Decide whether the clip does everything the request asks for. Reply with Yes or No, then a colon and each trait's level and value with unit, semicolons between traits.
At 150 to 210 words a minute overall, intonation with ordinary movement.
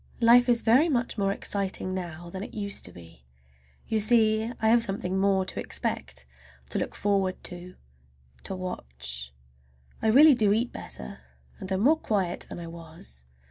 Yes: average, 170 wpm; average, 4.5 semitones